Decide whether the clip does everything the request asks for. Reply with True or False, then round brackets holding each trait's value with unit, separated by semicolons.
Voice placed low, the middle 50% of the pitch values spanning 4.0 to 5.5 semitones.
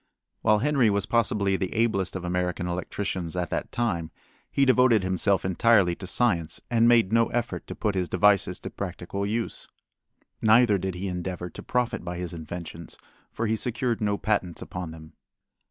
True (100 Hz; 4.3 semitones)